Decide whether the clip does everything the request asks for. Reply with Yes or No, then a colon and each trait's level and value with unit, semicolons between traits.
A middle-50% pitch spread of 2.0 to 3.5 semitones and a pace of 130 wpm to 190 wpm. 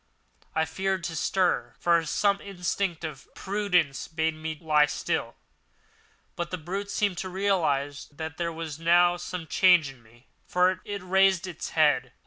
Yes: average, 3.2 semitones; average, 155 wpm